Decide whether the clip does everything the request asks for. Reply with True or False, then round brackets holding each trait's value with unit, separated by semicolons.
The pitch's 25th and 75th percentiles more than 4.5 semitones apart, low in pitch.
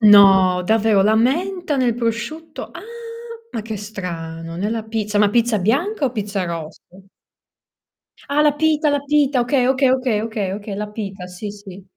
False (4.9 semitones; 220 Hz)